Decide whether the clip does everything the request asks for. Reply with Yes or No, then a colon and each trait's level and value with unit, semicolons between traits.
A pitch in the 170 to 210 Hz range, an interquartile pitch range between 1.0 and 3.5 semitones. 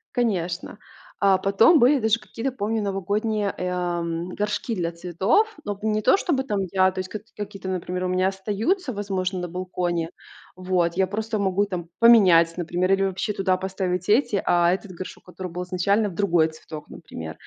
Yes: high, 190 Hz; average, 2.7 semitones